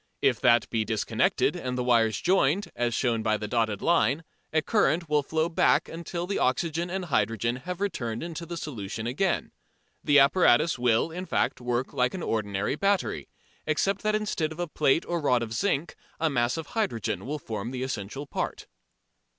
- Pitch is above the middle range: No, medium, 140 Hz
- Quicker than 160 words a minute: Yes, average, 185 wpm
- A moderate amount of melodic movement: No, wide, 6.4 semitones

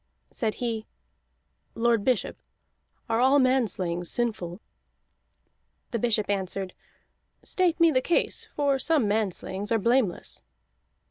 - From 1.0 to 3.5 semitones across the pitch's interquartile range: No, average, 4.3 semitones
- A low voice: No, high, 230 Hz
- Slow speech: Yes, slow, 110 wpm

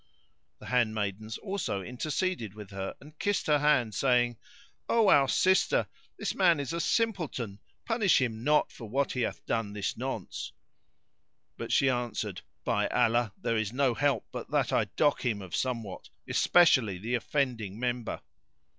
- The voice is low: Yes, low, 125 Hz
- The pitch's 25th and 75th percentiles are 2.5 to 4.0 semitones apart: No, average, 5.3 semitones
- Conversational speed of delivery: Yes, average, 155 wpm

